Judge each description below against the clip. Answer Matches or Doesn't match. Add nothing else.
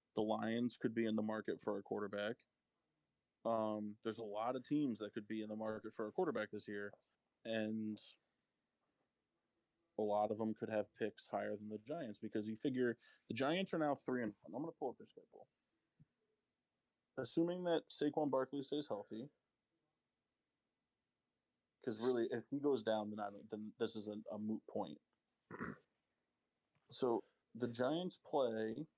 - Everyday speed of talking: Matches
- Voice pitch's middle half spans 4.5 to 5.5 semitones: Doesn't match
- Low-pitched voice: Matches